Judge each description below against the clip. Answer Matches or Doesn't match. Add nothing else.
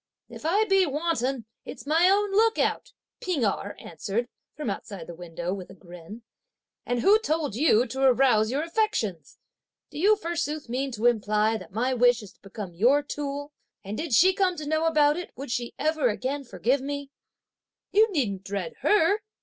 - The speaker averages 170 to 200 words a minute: Matches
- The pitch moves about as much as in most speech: Doesn't match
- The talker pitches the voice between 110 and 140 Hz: Doesn't match